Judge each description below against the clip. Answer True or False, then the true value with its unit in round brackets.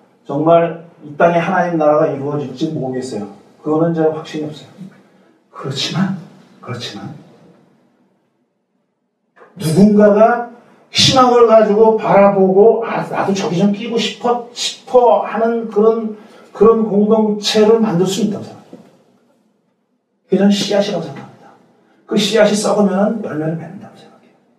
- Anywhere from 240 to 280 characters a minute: True (275 characters per minute)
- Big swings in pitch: False (4.7 semitones)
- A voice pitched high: True (205 Hz)